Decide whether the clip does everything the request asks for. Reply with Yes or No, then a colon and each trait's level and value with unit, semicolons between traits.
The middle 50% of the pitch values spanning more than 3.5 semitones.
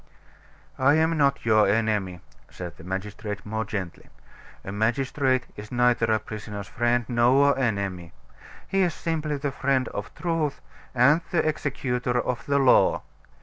Yes: average, 5.0 semitones